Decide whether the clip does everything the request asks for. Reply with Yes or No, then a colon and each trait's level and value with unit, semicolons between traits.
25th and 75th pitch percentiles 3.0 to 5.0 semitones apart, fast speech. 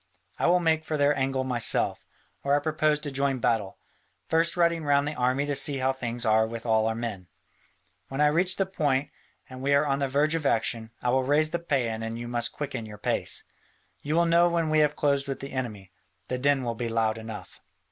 Yes: average, 4.3 semitones; fast, 230 wpm